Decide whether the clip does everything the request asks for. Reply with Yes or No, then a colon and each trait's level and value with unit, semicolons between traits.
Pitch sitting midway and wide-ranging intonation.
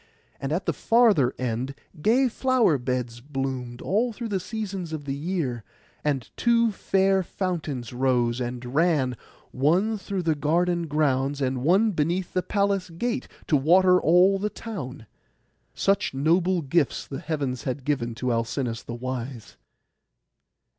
Yes: medium, 155 Hz; wide, 6.7 semitones